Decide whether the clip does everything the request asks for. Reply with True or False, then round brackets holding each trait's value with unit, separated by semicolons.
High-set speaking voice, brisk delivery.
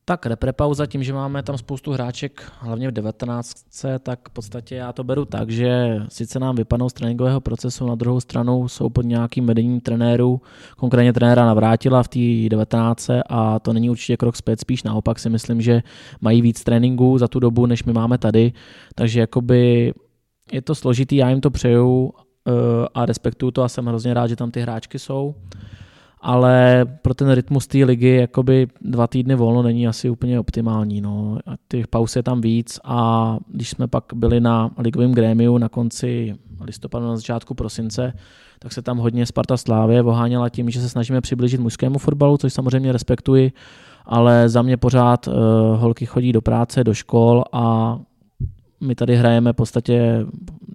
False (120 Hz; 175 wpm)